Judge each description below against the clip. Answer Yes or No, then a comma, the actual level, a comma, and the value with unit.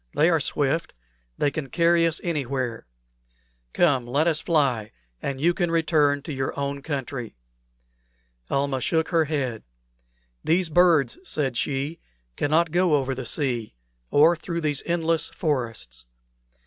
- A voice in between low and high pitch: Yes, medium, 145 Hz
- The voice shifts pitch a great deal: No, average, 3.7 semitones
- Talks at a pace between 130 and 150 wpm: Yes, slow, 135 wpm